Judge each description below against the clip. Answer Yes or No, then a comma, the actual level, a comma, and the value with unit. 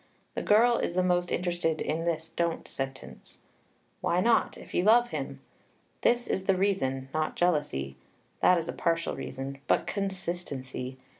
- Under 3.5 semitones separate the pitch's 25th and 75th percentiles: No, wide, 5.4 semitones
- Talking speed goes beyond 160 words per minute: No, average, 155 wpm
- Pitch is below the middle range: No, medium, 170 Hz